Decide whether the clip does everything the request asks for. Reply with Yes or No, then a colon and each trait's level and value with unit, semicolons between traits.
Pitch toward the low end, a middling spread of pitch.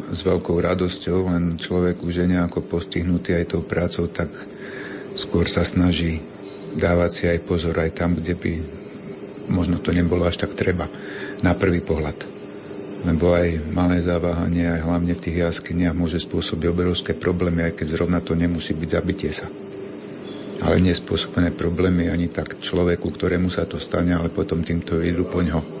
No: very low, 85 Hz; narrow, 1.3 semitones